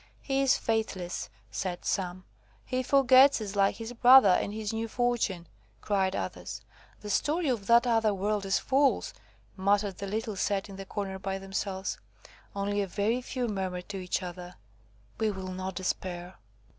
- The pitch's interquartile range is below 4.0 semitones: Yes, average, 3.1 semitones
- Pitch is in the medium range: No, high, 200 Hz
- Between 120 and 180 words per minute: Yes, average, 165 wpm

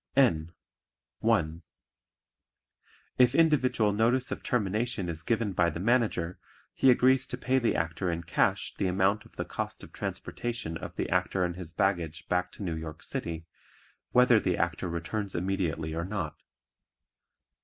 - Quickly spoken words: No, average, 155 wpm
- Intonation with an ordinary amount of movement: No, wide, 5.7 semitones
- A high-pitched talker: No, very low, 95 Hz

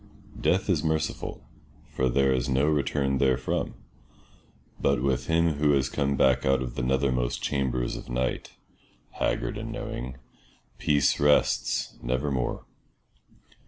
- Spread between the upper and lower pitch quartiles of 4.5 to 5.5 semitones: No, narrow, 2.4 semitones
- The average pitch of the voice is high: No, very low, 65 Hz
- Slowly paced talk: Yes, slow, 125 wpm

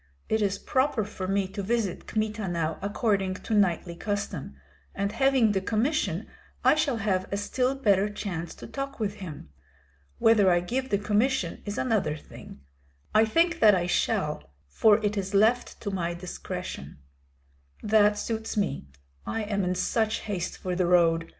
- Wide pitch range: No, average, 3.1 semitones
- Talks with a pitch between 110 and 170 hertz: No, high, 205 Hz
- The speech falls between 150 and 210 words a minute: Yes, average, 165 wpm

